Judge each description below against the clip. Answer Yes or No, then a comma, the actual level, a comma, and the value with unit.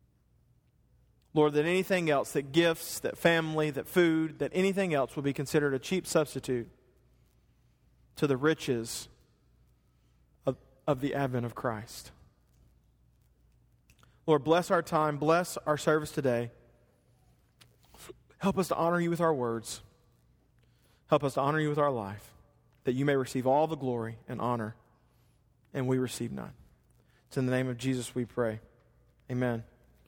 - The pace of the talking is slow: No, average, 150 wpm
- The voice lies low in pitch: Yes, low, 130 Hz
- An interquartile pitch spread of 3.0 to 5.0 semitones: Yes, average, 4.4 semitones